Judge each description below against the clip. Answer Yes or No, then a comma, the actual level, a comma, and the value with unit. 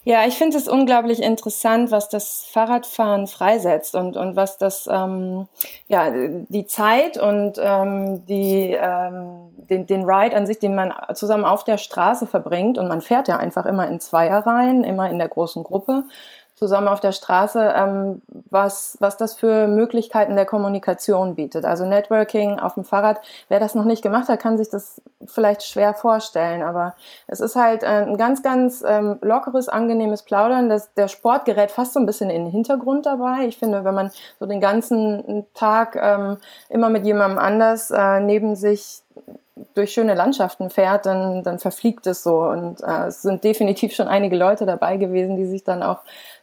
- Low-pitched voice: No, high, 205 Hz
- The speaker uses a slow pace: No, average, 180 wpm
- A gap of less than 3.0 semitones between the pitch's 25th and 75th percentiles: Yes, narrow, 2.6 semitones